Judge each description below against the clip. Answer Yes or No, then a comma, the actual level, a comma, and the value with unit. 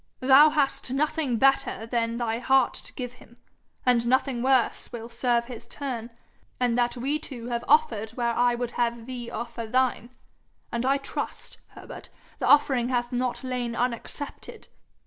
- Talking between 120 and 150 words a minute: No, average, 160 wpm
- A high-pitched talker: Yes, high, 245 Hz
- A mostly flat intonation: Yes, narrow, 1.9 semitones